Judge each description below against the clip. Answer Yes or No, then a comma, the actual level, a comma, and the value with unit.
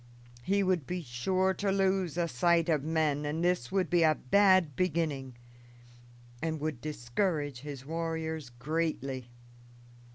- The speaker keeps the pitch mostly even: No, average, 4.1 semitones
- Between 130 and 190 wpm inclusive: Yes, slow, 135 wpm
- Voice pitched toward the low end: No, medium, 160 Hz